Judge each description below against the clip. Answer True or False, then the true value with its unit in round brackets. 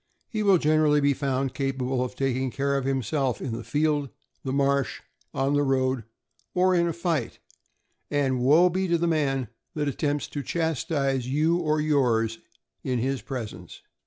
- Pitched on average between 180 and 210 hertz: False (140 Hz)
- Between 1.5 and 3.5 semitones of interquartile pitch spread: True (2.9 semitones)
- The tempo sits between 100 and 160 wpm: False (170 wpm)